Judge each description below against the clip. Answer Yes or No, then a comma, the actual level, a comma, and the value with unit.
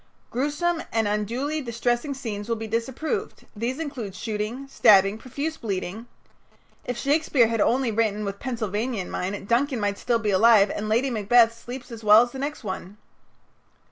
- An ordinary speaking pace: Yes, average, 170 wpm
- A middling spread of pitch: Yes, average, 3.8 semitones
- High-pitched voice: Yes, high, 230 Hz